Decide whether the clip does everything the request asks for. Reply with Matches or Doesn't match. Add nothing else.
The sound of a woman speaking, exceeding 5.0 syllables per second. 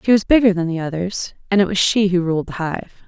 Matches